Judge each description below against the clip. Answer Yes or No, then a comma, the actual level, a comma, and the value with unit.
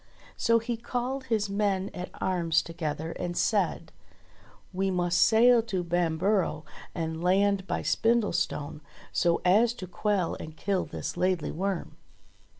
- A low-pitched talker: No, medium, 185 Hz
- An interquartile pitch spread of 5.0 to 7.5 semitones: No, average, 3.7 semitones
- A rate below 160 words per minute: Yes, slow, 135 wpm